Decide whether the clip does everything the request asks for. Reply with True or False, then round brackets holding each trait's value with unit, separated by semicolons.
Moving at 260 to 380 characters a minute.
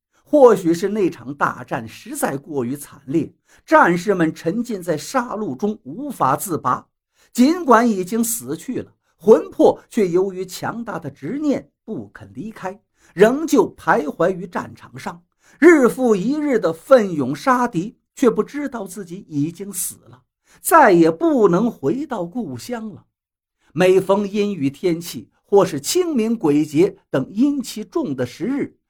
False (210 characters per minute)